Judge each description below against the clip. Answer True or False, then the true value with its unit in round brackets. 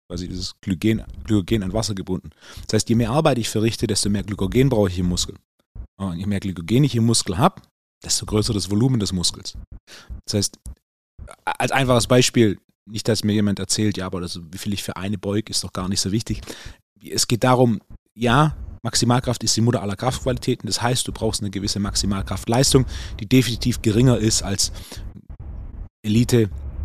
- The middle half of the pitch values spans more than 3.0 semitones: True (3.5 semitones)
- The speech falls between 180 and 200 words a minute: True (185 wpm)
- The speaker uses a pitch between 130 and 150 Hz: False (105 Hz)